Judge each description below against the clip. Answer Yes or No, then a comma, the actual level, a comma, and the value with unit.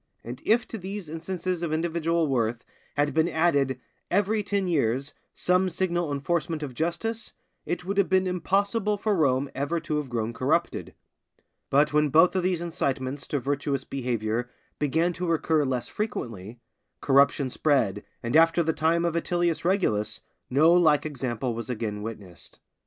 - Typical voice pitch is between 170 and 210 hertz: No, medium, 155 Hz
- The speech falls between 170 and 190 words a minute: No, average, 155 wpm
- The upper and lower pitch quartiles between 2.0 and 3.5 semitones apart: No, average, 5.0 semitones